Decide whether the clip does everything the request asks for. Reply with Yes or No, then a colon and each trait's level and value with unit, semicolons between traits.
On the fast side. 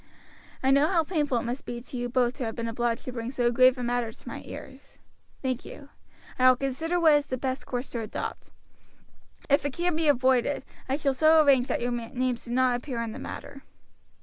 Yes: fast, 225 wpm